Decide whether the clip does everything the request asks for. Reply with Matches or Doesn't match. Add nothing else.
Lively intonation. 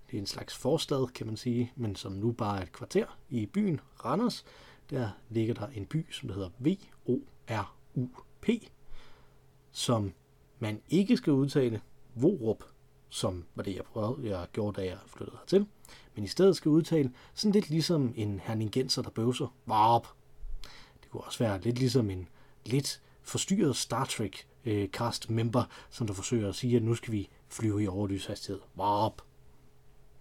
Doesn't match